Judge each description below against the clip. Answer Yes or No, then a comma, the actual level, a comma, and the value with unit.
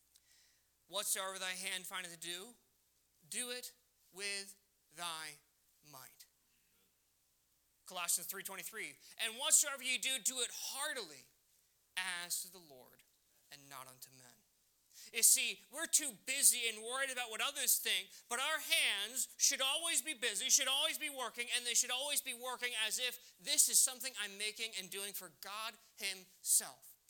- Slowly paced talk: No, average, 150 wpm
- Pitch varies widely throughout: Yes, wide, 6.7 semitones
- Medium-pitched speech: No, high, 205 Hz